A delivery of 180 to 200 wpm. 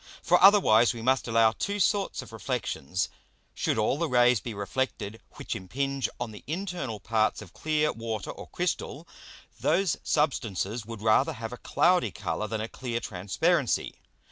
No: average, 160 wpm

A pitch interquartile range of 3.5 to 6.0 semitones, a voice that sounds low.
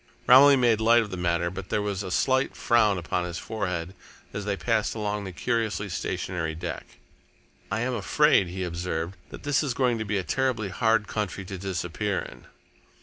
Yes: average, 4.3 semitones; low, 105 Hz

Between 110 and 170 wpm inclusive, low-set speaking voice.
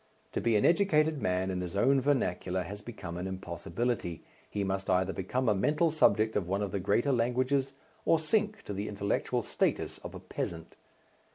No: average, 185 wpm; low, 105 Hz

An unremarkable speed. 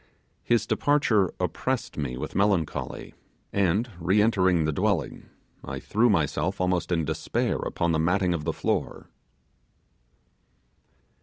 No: slow, 125 wpm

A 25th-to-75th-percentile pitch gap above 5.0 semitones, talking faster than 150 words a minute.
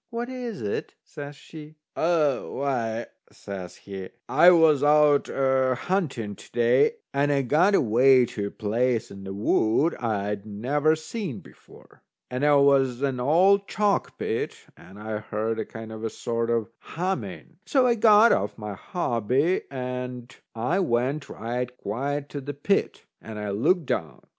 Yes: wide, 5.6 semitones; average, 160 wpm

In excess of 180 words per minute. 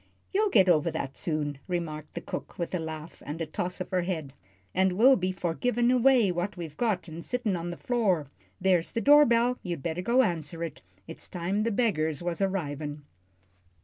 Yes: average, 200 wpm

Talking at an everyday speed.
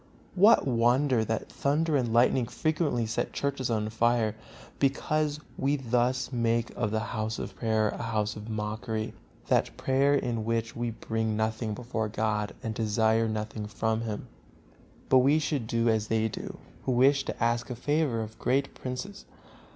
Yes: average, 170 wpm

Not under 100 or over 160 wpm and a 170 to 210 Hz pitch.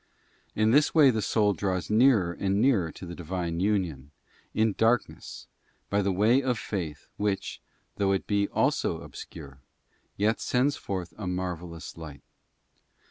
No: average, 145 wpm; low, 100 Hz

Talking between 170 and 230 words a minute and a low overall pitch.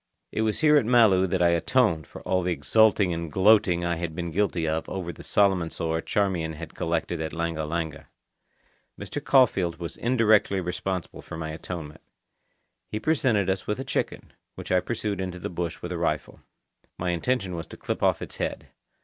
Yes: average, 190 wpm; very low, 90 Hz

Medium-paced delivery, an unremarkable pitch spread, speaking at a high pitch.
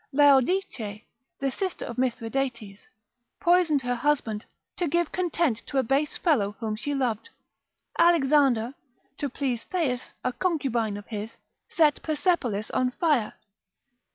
No: slow, 125 wpm; average, 5.0 semitones; very high, 270 Hz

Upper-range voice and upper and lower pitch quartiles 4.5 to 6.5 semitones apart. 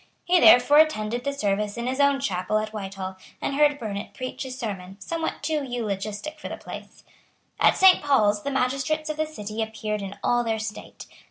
Yes: high, 235 Hz; average, 5.2 semitones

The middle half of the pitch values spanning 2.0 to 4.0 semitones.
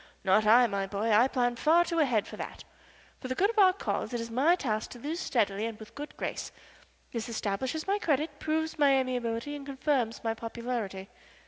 No: average, 4.7 semitones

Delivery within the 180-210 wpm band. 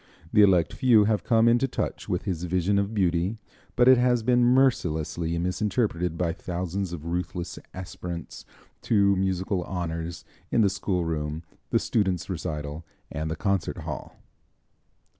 No: average, 140 wpm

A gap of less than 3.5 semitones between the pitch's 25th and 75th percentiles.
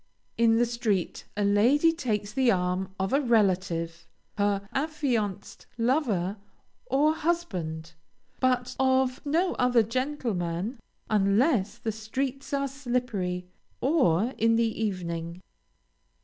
No: wide, 5.5 semitones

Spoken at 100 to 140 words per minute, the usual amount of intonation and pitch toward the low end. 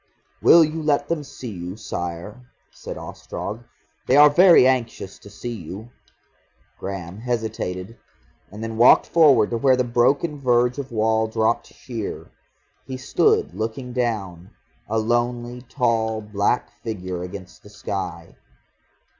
Yes: slow, 135 wpm; average, 3.7 semitones; low, 115 Hz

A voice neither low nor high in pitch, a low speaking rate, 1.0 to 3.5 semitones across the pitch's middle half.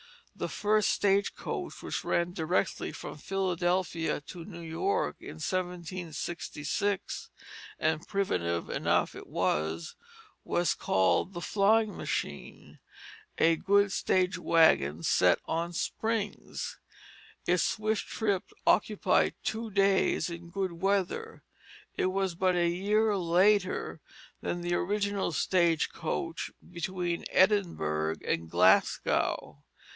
Yes: medium, 180 Hz; slow, 110 wpm; average, 3.1 semitones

